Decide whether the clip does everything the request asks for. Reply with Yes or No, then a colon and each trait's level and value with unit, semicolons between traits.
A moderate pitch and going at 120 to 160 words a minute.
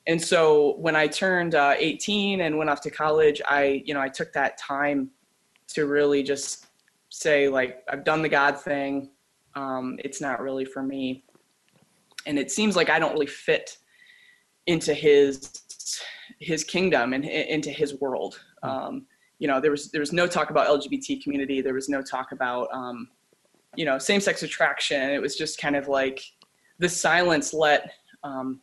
No: medium, 145 Hz; average, 175 wpm